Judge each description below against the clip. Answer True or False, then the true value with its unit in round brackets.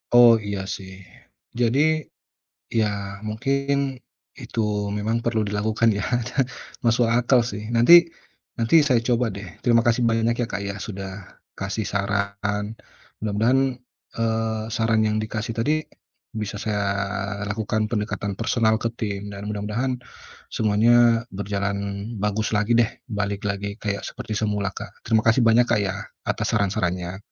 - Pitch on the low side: True (110 Hz)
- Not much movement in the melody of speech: True (2.2 semitones)